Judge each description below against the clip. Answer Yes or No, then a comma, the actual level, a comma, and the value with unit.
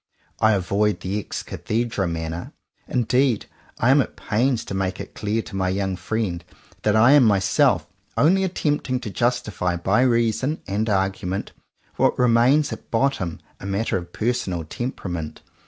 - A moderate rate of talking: Yes, average, 155 wpm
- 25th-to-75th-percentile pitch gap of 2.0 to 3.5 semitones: No, average, 4.6 semitones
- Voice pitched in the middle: No, low, 105 Hz